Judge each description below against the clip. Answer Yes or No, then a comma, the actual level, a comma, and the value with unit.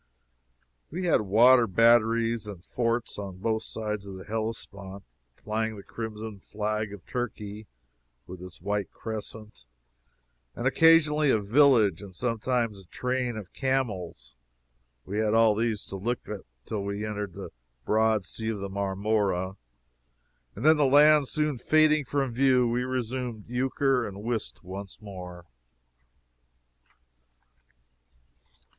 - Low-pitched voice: Yes, low, 110 Hz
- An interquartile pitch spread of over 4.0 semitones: No, average, 3.7 semitones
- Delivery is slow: Yes, slow, 130 wpm